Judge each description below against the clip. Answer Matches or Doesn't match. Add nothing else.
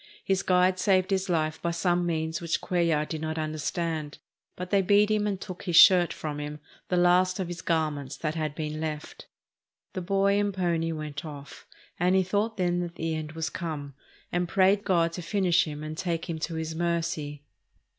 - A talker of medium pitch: Matches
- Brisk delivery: Doesn't match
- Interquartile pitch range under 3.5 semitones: Matches